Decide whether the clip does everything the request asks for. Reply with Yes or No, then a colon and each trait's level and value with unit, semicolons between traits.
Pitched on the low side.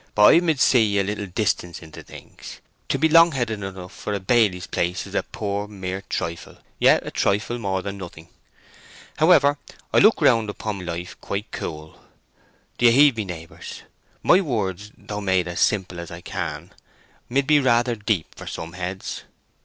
Yes: low, 100 Hz